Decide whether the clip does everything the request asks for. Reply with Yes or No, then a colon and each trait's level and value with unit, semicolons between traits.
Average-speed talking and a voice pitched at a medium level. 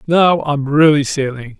Yes: average, 150 wpm; medium, 145 Hz